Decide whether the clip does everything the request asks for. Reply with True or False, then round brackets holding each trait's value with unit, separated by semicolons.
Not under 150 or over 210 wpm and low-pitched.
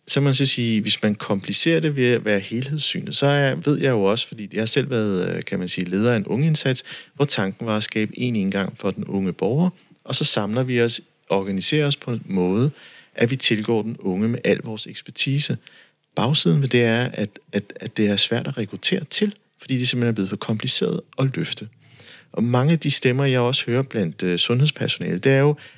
False (220 wpm; 120 Hz)